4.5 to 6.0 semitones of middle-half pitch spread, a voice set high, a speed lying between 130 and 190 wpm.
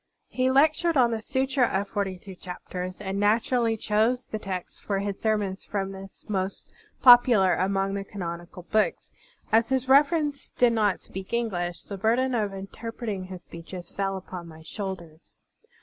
No: average, 3.9 semitones; high, 200 Hz; average, 160 wpm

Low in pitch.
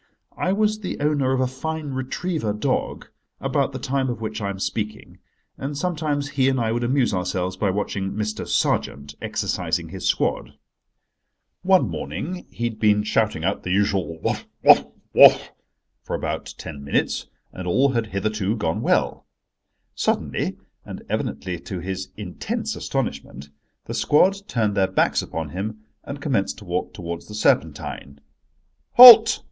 Yes: low, 110 Hz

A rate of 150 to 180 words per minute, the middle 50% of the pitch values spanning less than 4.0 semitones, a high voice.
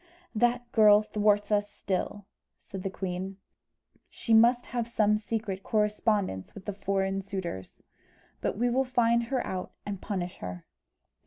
No: average, 140 wpm; average, 3.1 semitones; high, 205 Hz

